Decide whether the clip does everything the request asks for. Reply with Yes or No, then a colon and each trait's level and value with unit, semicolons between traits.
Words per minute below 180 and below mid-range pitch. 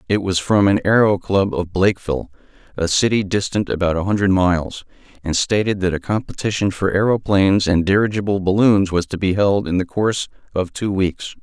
No: average, 185 wpm; very low, 95 Hz